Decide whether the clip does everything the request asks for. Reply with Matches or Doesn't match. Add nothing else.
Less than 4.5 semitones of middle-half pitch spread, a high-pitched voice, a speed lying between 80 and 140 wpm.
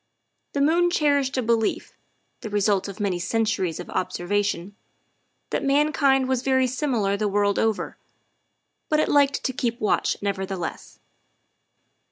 Doesn't match